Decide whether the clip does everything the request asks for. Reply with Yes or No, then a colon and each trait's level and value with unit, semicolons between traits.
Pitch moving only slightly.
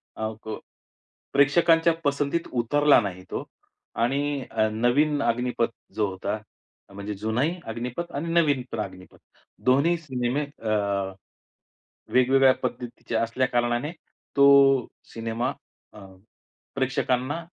No: average, 4.2 semitones